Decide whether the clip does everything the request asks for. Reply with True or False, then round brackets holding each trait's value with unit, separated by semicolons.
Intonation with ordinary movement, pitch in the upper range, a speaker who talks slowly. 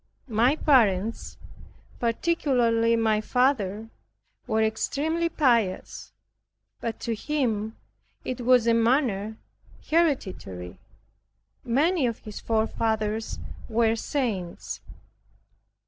True (3.2 semitones; 230 Hz; 85 wpm)